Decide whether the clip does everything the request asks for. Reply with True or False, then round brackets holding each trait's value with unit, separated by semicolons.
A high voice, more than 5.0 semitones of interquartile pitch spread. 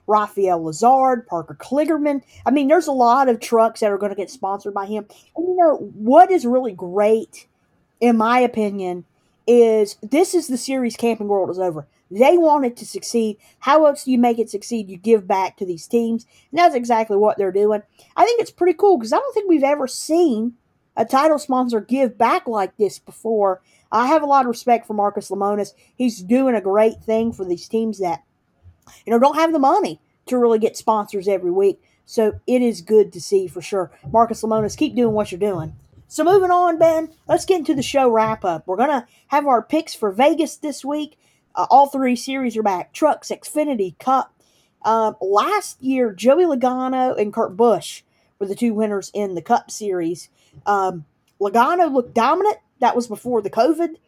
True (230 Hz; 5.4 semitones)